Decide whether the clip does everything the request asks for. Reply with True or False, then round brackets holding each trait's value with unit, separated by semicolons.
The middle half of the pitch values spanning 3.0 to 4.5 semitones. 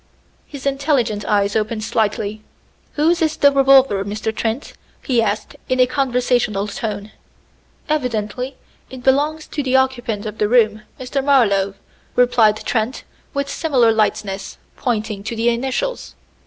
True (4.0 semitones)